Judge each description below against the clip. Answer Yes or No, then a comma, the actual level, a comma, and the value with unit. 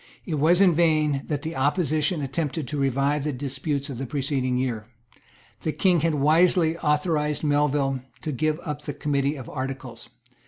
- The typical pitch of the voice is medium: Yes, medium, 145 Hz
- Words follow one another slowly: No, average, 165 wpm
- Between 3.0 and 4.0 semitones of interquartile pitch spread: No, narrow, 2.4 semitones